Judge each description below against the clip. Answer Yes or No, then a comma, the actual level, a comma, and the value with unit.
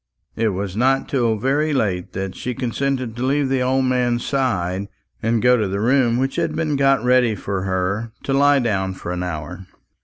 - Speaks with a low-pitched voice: Yes, low, 120 Hz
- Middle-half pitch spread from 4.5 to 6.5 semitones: Yes, average, 5.3 semitones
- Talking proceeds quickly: No, average, 195 wpm